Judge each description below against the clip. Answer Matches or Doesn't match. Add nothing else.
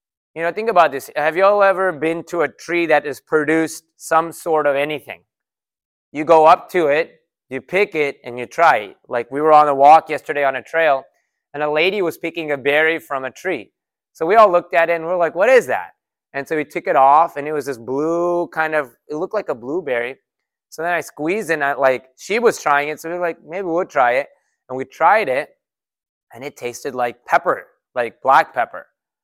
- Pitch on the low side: Doesn't match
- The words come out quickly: Matches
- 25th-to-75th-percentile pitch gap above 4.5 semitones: Doesn't match